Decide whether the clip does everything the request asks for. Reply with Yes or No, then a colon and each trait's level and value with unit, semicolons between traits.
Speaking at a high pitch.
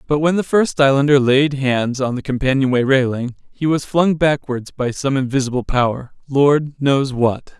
No: low, 135 Hz